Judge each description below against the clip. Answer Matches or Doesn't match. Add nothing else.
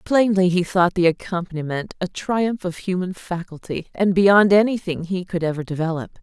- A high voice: Doesn't match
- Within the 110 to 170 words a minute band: Matches